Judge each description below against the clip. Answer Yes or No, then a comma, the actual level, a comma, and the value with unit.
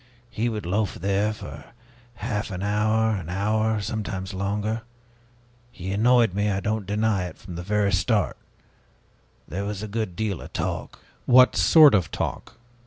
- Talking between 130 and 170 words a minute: Yes, average, 160 wpm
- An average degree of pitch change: No, narrow, 2.2 semitones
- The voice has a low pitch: Yes, low, 105 Hz